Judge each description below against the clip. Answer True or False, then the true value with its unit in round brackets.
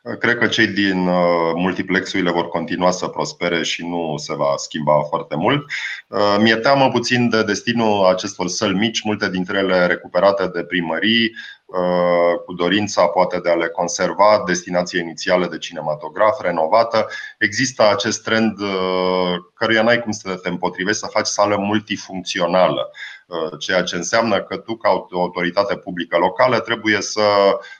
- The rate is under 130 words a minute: False (140 wpm)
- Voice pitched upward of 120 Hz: False (95 Hz)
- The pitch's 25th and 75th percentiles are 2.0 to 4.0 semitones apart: True (3.4 semitones)